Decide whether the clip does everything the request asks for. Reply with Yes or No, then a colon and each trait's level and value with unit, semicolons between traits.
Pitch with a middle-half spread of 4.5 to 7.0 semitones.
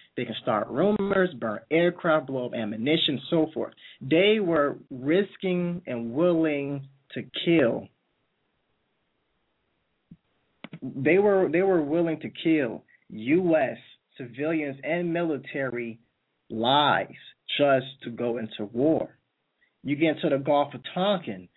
Yes: average, 5.2 semitones